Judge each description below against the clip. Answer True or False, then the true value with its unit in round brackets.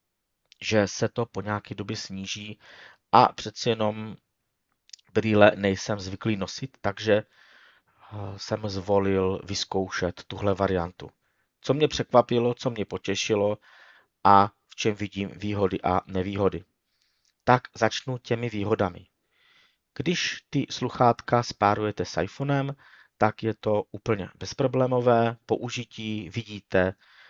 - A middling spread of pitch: True (3.3 semitones)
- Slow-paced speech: True (110 wpm)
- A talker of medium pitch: False (105 Hz)